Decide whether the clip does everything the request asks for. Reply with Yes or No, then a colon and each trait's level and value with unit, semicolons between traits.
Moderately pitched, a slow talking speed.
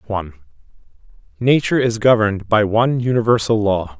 No: low, 110 Hz; slow, 120 wpm